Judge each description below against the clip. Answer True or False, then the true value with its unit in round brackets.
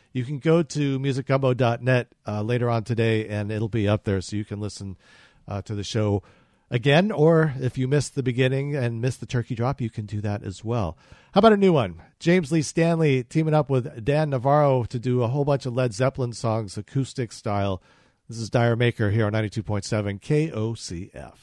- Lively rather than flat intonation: False (4.3 semitones)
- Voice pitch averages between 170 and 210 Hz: False (120 Hz)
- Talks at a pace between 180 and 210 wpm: True (200 wpm)